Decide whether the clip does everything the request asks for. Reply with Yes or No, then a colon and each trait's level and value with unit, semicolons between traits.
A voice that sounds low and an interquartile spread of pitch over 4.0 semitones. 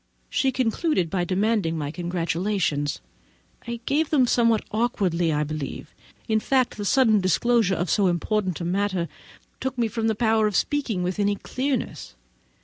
No: high, 205 Hz; average, 5.1 semitones